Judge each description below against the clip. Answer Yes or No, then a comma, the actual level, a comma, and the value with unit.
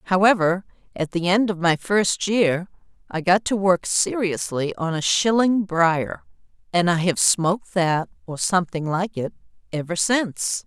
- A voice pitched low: No, medium, 185 Hz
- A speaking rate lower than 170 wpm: Yes, average, 160 wpm